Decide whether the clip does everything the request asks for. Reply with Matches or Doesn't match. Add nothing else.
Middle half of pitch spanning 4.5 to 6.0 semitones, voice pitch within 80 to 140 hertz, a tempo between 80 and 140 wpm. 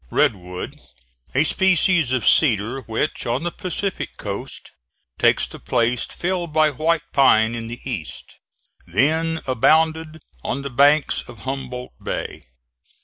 Matches